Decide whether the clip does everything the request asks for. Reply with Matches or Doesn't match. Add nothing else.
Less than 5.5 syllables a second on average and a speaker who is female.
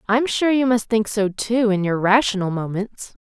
Matches